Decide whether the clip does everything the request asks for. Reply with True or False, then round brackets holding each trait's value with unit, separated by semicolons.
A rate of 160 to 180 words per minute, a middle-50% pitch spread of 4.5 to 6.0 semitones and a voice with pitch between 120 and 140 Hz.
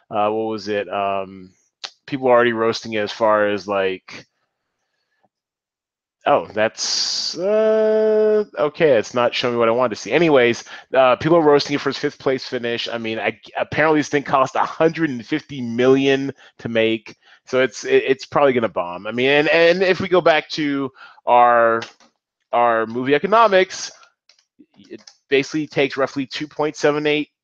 True (175 wpm; 5.1 semitones; 135 Hz)